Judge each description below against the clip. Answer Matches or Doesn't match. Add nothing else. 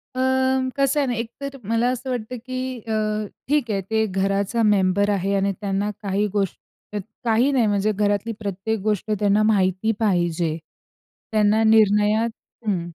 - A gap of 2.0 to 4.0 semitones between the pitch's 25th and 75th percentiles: Matches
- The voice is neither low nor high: Doesn't match